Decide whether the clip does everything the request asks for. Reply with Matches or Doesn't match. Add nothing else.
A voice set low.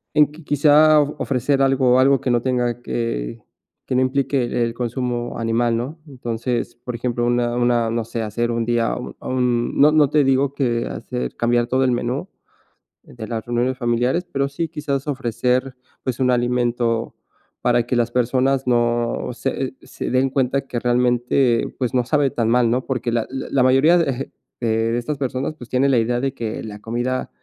Matches